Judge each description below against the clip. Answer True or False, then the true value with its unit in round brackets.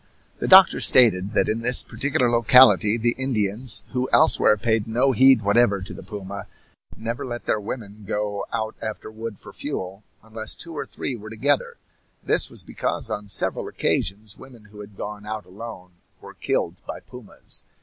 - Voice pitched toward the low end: True (110 Hz)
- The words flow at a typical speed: True (170 wpm)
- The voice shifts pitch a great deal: False (2.9 semitones)